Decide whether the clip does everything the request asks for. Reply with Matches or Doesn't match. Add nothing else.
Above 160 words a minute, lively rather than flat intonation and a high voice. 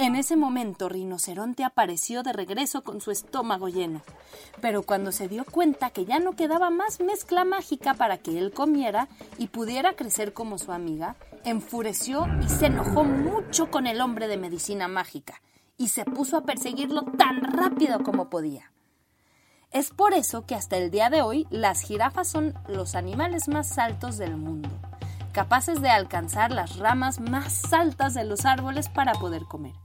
Matches